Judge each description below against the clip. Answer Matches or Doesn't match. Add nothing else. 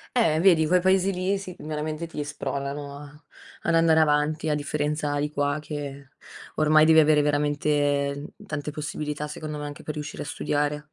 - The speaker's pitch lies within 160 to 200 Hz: Doesn't match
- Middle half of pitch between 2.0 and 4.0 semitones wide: Doesn't match